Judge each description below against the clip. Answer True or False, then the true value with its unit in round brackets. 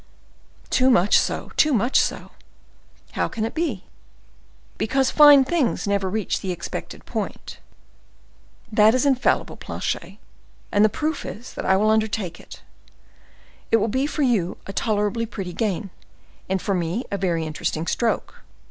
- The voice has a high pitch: True (215 Hz)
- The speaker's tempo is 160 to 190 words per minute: False (145 wpm)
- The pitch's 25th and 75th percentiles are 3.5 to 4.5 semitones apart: False (5.0 semitones)